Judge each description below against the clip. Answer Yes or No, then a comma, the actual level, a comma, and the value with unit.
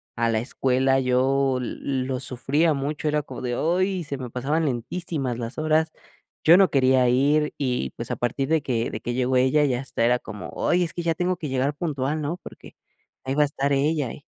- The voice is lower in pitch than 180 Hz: Yes, low, 135 Hz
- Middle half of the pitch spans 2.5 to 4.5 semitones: Yes, average, 3.3 semitones